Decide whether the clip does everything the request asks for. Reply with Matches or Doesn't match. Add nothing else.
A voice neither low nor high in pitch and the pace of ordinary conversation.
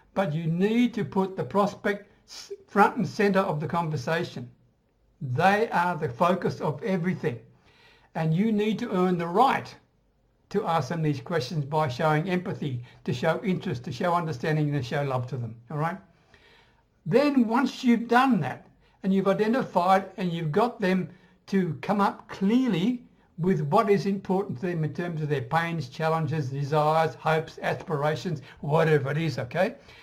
Matches